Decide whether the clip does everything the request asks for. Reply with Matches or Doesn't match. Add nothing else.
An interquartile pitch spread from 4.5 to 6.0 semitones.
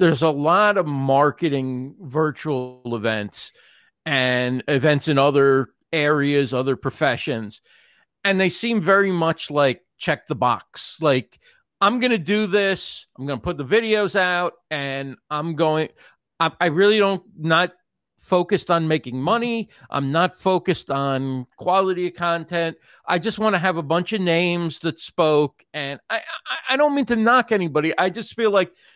Matches